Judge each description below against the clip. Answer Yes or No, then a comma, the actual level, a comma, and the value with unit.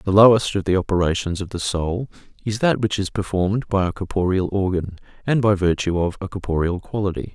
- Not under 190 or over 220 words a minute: Yes, average, 195 wpm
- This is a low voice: Yes, very low, 95 Hz